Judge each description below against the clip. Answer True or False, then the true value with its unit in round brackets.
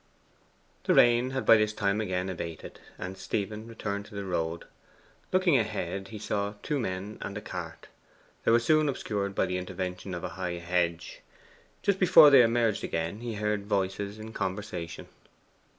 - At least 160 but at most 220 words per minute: True (165 wpm)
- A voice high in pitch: False (100 Hz)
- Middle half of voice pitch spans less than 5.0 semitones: True (3.6 semitones)